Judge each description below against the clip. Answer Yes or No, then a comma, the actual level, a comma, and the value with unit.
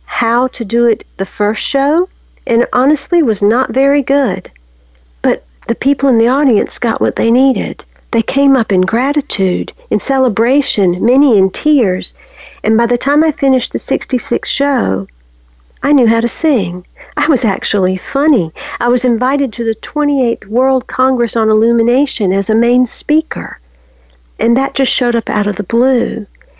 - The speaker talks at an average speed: Yes, average, 165 wpm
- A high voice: Yes, high, 240 Hz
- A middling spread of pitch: Yes, average, 4.6 semitones